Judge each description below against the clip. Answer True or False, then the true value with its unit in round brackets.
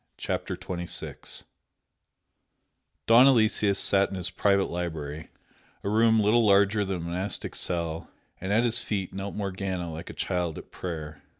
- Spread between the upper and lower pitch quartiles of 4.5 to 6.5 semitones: False (3.3 semitones)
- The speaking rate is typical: True (145 wpm)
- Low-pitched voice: True (95 Hz)